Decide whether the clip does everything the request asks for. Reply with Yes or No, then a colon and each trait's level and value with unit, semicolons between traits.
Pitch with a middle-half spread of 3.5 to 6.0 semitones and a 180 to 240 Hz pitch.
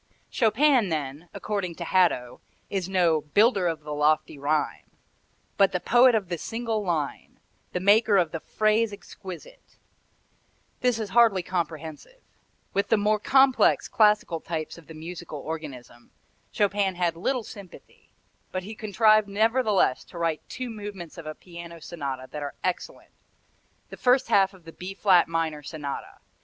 Yes: average, 4.9 semitones; medium, 185 Hz